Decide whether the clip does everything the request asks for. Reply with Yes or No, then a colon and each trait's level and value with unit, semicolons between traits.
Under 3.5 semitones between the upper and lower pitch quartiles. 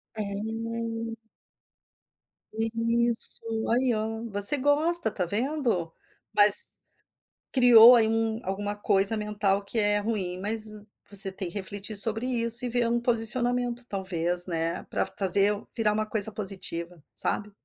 Yes: narrow, 2.6 semitones